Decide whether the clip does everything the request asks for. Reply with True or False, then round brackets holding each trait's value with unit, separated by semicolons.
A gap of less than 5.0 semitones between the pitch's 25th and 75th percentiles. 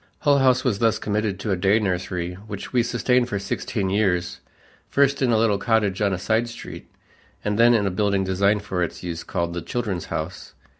True (3.6 semitones)